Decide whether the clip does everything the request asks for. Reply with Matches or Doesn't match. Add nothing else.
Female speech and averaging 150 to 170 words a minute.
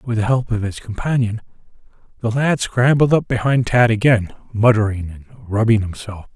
Doesn't match